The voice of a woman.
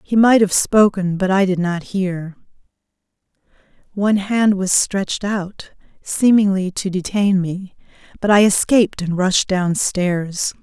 Yes: female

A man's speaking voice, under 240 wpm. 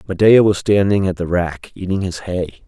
Yes: male; average, 200 wpm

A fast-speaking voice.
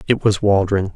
No: average, 190 wpm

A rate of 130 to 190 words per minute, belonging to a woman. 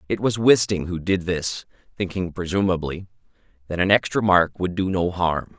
No: average, 170 wpm; male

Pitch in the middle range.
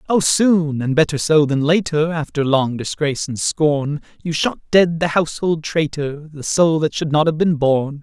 Yes: medium, 155 Hz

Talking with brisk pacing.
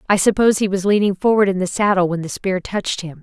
Yes: fast, 260 wpm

